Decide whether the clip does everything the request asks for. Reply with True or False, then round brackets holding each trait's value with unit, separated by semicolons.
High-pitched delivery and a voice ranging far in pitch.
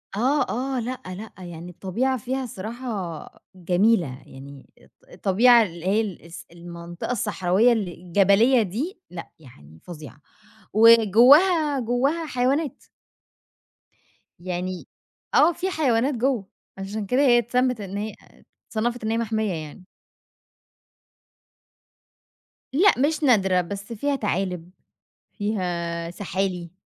True (210 Hz; 5.8 semitones)